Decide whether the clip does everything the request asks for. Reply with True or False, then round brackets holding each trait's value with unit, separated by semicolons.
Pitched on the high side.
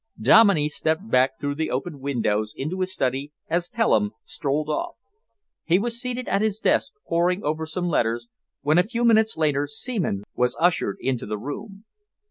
False (160 Hz)